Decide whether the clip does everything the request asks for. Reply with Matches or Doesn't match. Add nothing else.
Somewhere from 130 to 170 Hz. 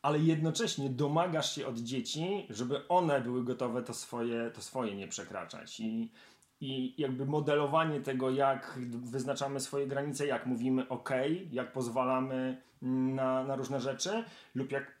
Matches